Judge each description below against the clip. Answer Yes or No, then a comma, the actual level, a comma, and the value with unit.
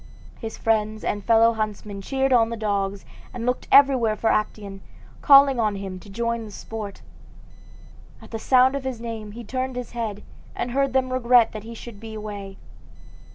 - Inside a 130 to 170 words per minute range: No, average, 180 wpm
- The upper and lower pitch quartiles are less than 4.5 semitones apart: Yes, average, 2.9 semitones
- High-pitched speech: Yes, high, 225 Hz